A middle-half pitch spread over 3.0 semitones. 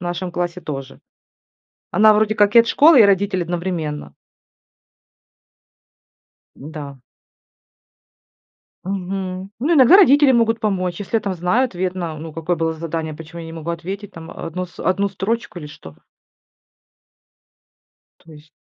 Yes: average, 4.1 semitones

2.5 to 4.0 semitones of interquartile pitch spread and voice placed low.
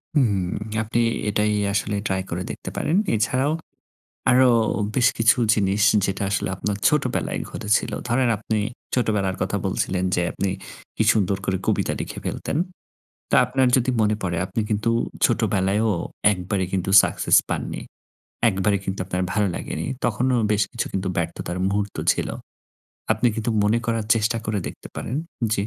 Yes: average, 3.3 semitones; low, 105 Hz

